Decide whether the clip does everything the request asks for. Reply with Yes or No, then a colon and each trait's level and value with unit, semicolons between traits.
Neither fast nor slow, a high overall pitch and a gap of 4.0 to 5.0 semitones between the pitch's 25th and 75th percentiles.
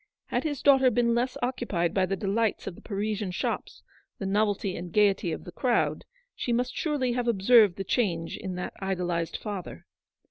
Yes: average, 180 wpm; high, 205 Hz; average, 4.6 semitones